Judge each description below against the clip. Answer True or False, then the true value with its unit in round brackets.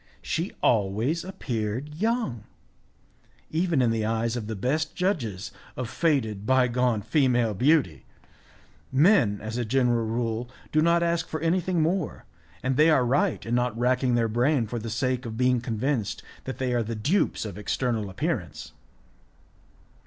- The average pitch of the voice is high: False (125 Hz)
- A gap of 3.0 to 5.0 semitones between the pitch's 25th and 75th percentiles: False (5.5 semitones)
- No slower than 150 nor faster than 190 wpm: True (155 wpm)